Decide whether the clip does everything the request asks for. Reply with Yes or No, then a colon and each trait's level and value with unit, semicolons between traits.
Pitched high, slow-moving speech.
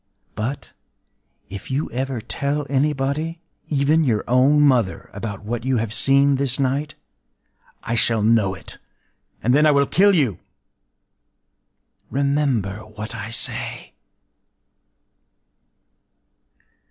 No: low, 130 Hz; slow, 105 wpm